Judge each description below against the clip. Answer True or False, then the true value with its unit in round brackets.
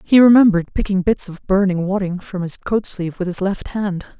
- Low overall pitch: False (190 Hz)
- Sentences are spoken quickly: True (215 wpm)